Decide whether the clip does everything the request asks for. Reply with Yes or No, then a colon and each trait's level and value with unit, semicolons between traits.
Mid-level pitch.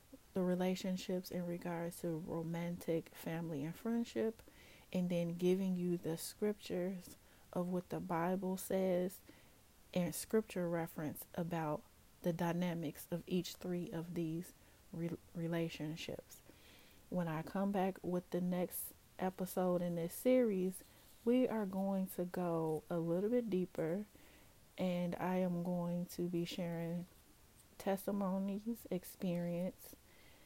Yes: medium, 180 Hz